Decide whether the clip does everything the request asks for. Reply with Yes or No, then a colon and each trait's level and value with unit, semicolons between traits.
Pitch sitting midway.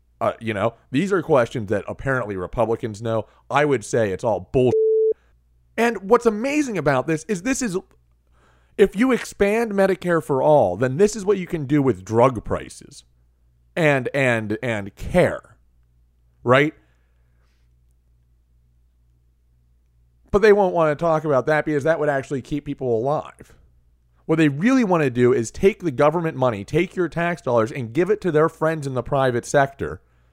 No: low, 130 Hz